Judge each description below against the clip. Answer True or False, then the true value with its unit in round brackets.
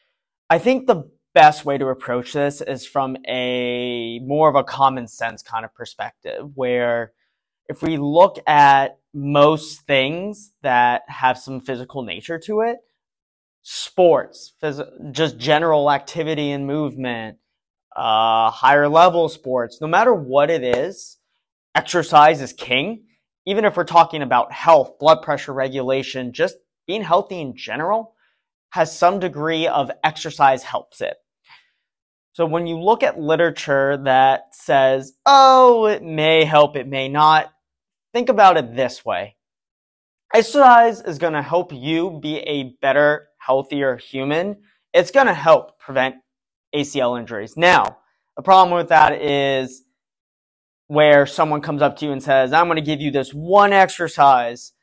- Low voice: False (145 Hz)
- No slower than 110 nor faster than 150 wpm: True (145 wpm)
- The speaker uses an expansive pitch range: False (4.2 semitones)